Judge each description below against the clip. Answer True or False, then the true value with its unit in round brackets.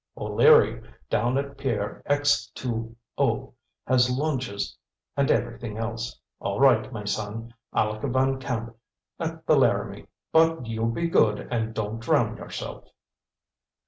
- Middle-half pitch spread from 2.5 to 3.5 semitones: True (3.2 semitones)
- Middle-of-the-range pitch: False (115 Hz)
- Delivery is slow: True (130 wpm)